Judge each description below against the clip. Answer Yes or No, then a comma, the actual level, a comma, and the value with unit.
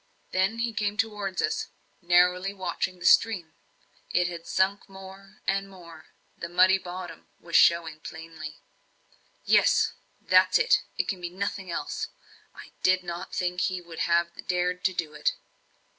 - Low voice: No, medium, 180 Hz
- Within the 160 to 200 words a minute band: No, average, 150 wpm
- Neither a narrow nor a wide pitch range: No, narrow, 2.2 semitones